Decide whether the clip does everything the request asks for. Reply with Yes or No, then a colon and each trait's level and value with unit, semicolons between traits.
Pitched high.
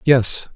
No: low, 125 Hz